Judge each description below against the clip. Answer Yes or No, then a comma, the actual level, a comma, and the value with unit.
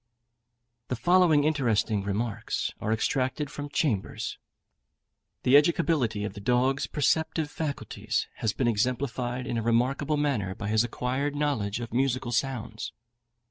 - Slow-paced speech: Yes, slow, 130 wpm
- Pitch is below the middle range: Yes, low, 125 Hz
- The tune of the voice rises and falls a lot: No, average, 4.5 semitones